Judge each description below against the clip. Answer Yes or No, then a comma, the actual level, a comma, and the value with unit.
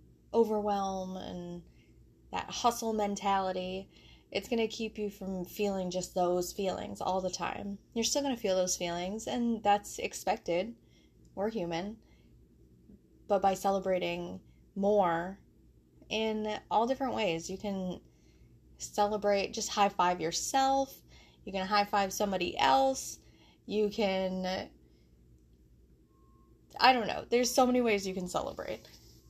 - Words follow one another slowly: Yes, slow, 130 wpm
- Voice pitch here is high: Yes, high, 195 Hz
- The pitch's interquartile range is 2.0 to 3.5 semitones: Yes, average, 3.1 semitones